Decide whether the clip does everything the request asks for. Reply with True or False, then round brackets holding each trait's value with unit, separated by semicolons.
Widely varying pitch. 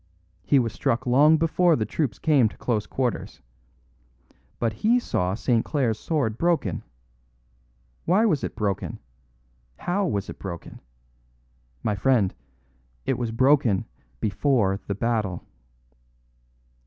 True (6.2 semitones)